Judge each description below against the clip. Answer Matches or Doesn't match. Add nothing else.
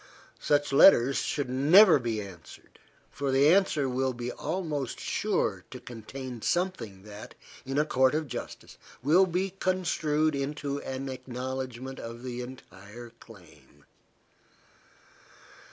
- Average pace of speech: Doesn't match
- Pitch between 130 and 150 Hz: Matches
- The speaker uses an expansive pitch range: Doesn't match